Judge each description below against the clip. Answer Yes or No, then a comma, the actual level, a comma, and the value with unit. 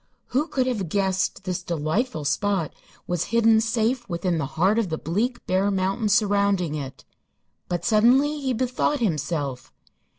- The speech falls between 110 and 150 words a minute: Yes, average, 145 wpm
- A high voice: Yes, high, 200 Hz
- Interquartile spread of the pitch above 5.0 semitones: Yes, wide, 5.4 semitones